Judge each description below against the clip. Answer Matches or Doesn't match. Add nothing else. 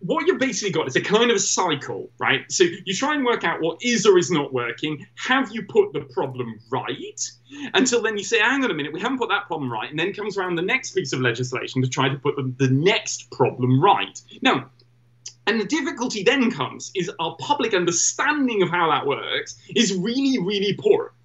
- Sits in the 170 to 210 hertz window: Matches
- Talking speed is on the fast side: Matches